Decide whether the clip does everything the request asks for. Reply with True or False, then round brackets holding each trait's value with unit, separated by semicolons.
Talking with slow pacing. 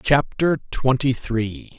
True (100 wpm)